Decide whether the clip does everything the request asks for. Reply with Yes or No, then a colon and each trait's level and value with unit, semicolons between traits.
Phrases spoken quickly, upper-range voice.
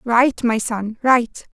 No: average, 155 wpm; high, 235 Hz